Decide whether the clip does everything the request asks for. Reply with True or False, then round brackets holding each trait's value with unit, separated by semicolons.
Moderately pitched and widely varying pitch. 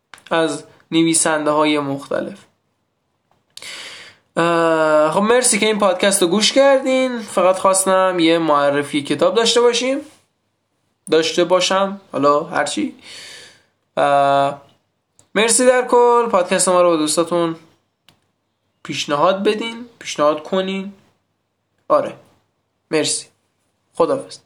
True (180 Hz; 6.6 semitones)